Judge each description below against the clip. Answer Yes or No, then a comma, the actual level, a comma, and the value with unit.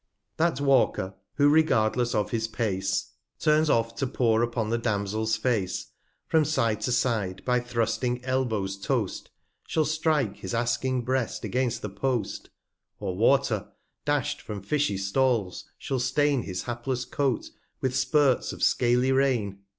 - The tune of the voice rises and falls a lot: No, average, 3.5 semitones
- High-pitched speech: No, low, 120 Hz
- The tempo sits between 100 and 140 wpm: No, average, 155 wpm